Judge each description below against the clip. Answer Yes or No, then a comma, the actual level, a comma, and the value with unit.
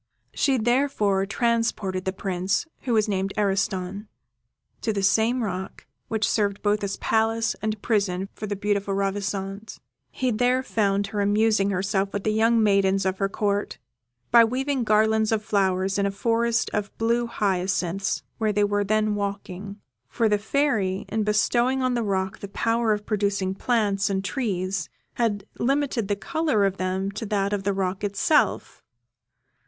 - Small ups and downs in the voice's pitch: Yes, narrow, 2.3 semitones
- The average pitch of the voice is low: No, high, 205 Hz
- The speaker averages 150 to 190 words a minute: Yes, average, 160 wpm